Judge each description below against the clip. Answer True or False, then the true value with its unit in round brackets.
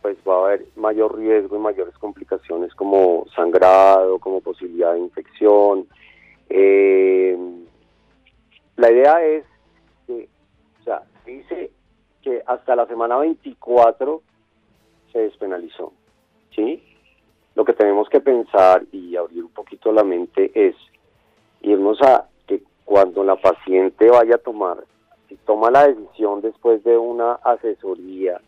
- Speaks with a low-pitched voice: True (110 Hz)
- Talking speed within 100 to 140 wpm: True (125 wpm)